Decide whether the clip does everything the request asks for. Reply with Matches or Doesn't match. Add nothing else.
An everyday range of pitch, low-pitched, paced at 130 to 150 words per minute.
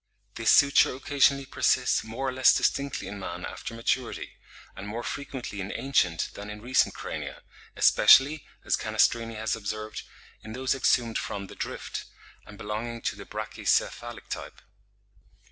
Matches